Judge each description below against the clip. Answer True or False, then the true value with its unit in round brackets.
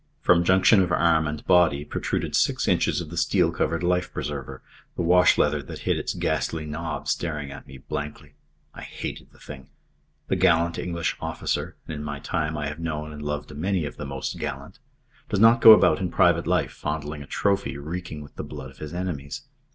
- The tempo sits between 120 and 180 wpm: False (200 wpm)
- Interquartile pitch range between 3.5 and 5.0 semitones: False (3.1 semitones)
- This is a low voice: True (80 Hz)